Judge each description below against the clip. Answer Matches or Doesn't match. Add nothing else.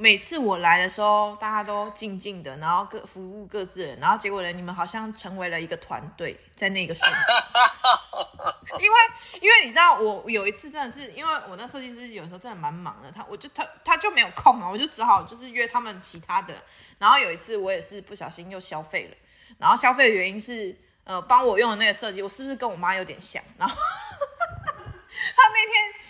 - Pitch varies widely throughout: Matches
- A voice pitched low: Doesn't match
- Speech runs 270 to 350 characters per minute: Matches